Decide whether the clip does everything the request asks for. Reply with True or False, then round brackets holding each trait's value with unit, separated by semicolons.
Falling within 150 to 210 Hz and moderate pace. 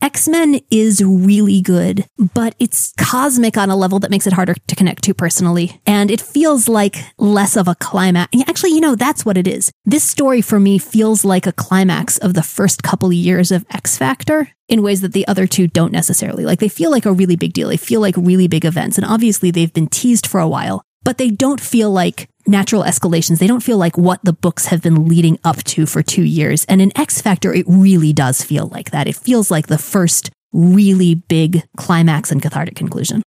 False (190 Hz; 225 wpm)